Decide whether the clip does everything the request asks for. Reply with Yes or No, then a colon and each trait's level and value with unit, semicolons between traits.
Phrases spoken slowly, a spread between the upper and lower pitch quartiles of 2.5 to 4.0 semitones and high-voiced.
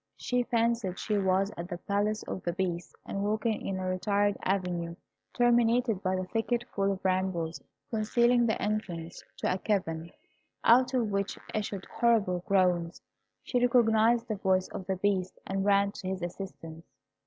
No: average, 165 wpm; average, 3.3 semitones; high, 200 Hz